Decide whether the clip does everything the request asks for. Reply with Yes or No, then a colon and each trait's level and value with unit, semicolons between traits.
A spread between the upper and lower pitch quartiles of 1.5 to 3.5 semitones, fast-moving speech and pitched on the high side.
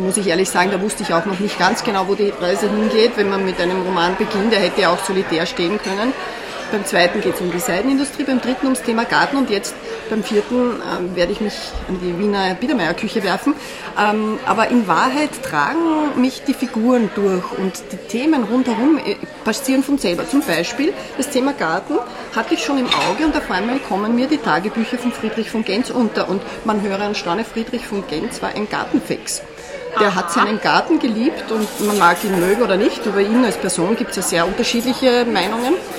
No: average, 4.7 semitones; fast, 205 wpm; high, 220 Hz